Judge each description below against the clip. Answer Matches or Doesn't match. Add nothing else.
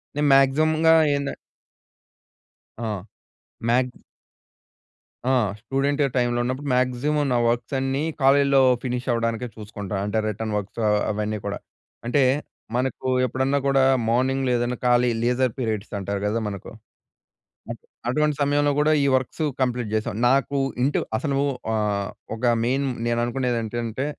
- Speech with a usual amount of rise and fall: Matches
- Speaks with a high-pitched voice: Doesn't match